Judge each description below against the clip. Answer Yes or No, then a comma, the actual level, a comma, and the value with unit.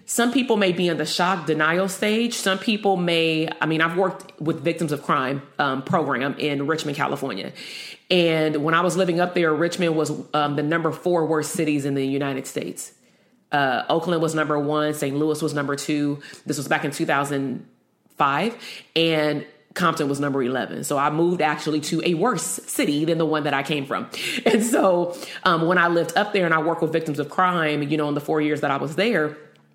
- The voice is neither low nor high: Yes, medium, 160 Hz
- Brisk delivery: Yes, fast, 210 wpm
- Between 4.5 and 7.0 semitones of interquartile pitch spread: No, average, 2.8 semitones